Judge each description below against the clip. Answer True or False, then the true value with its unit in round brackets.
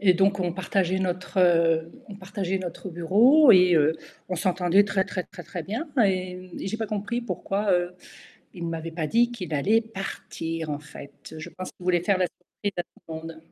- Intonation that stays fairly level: False (3.0 semitones)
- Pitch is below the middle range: False (185 Hz)